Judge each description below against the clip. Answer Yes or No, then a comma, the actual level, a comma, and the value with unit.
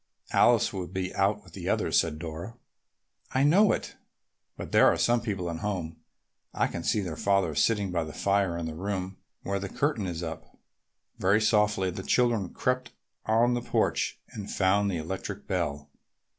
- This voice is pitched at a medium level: No, very low, 95 Hz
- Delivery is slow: No, average, 180 wpm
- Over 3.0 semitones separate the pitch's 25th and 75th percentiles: Yes, average, 3.6 semitones